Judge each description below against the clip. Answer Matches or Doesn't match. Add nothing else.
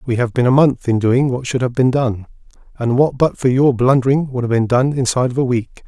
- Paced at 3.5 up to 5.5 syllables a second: Doesn't match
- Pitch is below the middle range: Matches